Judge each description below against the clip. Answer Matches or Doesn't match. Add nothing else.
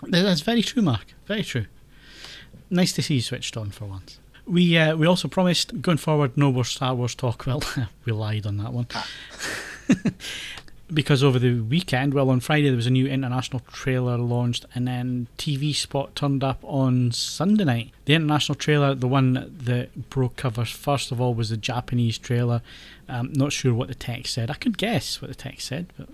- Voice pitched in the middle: Doesn't match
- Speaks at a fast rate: Doesn't match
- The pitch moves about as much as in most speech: Matches